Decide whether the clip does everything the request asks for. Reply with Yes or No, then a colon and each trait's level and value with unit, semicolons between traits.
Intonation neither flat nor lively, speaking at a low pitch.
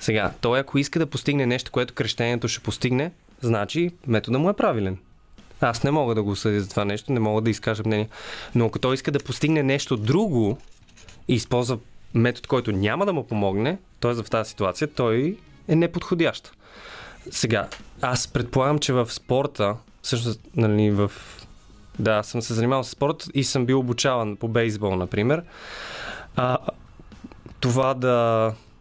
Yes: average, 4.1 semitones; low, 120 Hz